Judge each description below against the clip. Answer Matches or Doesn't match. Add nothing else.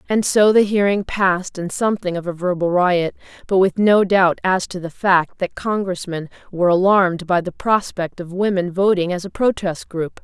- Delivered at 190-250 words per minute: Matches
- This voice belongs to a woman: Matches